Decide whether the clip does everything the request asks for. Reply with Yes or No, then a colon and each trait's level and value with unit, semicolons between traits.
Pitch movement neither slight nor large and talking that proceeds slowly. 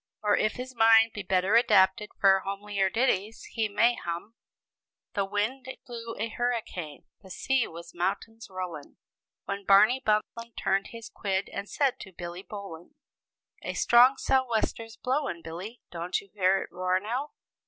No: average, 3.5 semitones; average, 155 wpm